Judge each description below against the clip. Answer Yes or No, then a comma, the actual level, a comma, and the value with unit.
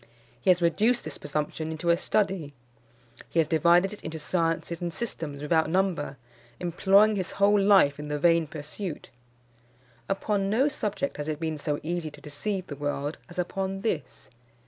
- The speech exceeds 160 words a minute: Yes, average, 170 wpm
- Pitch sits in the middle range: Yes, medium, 170 Hz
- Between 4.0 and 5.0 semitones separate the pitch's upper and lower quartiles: Yes, average, 4.3 semitones